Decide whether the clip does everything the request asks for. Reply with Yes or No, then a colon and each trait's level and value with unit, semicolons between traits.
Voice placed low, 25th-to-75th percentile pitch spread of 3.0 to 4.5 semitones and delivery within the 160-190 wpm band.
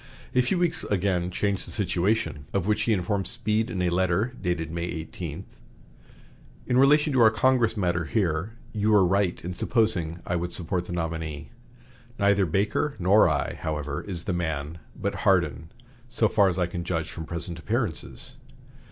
Yes: very low, 90 Hz; average, 4.1 semitones; average, 170 wpm